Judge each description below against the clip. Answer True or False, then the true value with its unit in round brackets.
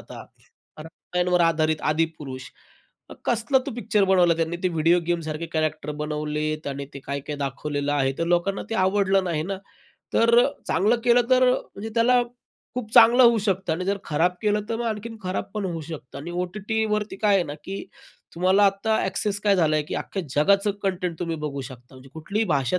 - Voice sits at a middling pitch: True (180 Hz)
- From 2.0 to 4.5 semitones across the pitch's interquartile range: False (5.1 semitones)